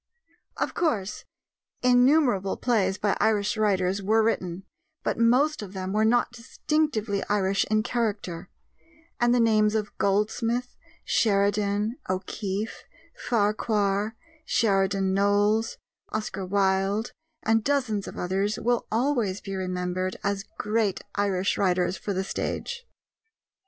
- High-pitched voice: Yes, high, 210 Hz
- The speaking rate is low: Yes, slow, 115 wpm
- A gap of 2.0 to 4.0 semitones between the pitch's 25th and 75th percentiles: Yes, average, 2.8 semitones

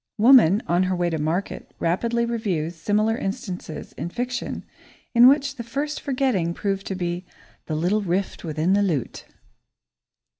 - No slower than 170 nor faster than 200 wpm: No, average, 150 wpm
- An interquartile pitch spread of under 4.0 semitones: No, wide, 5.4 semitones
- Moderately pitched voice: No, high, 195 Hz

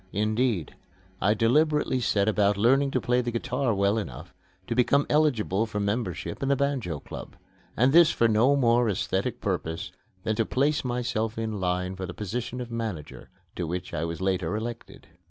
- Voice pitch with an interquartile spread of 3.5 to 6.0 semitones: Yes, average, 4.5 semitones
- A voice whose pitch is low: Yes, low, 110 Hz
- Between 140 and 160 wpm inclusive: No, average, 175 wpm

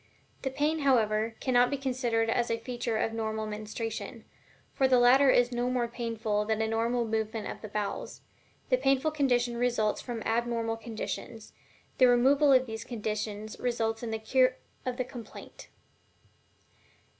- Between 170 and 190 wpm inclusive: No, average, 155 wpm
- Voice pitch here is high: Yes, high, 235 Hz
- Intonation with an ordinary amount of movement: No, narrow, 2.3 semitones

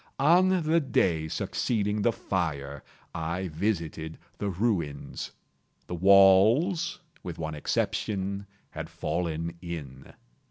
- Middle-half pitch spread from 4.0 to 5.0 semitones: No, wide, 5.4 semitones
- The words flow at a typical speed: No, slow, 105 wpm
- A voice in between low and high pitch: No, very low, 95 Hz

